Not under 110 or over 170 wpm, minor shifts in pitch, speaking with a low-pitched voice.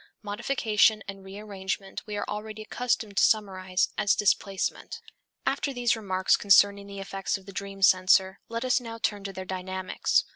No: average, 160 wpm; narrow, 2.0 semitones; high, 200 Hz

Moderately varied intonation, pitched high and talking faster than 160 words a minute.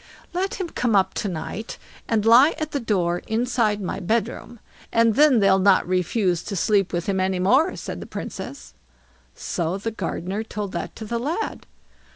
Yes: average, 4.0 semitones; high, 210 Hz; average, 180 wpm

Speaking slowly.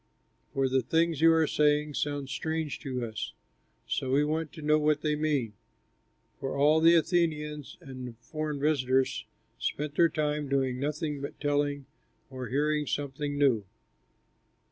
No: average, 150 wpm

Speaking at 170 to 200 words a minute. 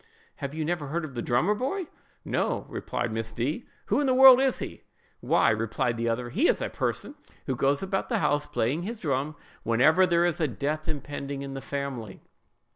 Yes: average, 195 wpm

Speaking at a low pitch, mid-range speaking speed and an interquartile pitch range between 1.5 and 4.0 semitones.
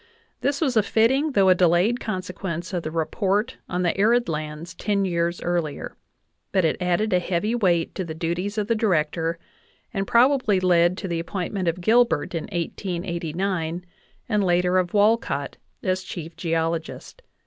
No: medium, 180 Hz; average, 170 wpm; average, 3.5 semitones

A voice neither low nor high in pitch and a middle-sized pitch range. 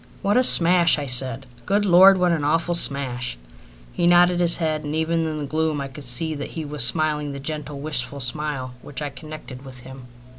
Yes: medium, 150 Hz; average, 3.5 semitones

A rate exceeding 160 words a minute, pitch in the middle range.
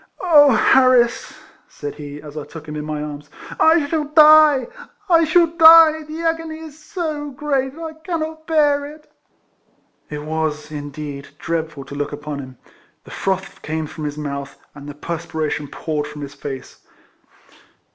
Yes: average, 170 wpm; medium, 170 Hz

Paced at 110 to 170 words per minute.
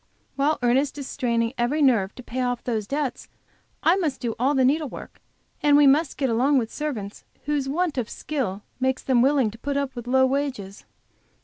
No: average, 195 wpm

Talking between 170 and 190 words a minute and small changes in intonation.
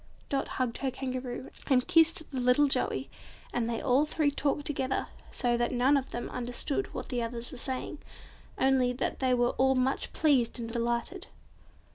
Yes: average, 175 wpm; narrow, 2.2 semitones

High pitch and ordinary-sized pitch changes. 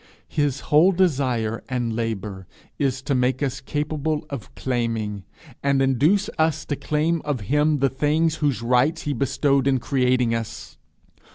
No: low, 135 Hz; average, 3.5 semitones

